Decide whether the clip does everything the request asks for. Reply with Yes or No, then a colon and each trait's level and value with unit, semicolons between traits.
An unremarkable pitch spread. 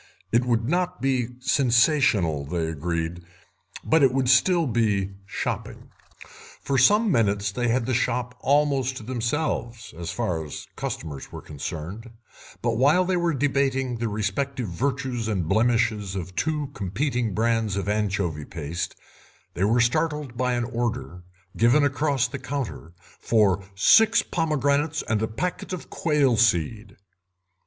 No: wide, 5.7 semitones